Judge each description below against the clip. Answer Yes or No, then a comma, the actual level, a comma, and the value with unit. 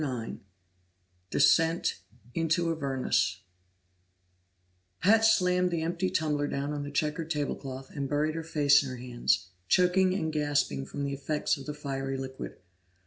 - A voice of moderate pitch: Yes, medium, 150 Hz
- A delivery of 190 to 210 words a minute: No, average, 145 wpm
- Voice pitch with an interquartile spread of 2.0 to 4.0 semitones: Yes, average, 3.4 semitones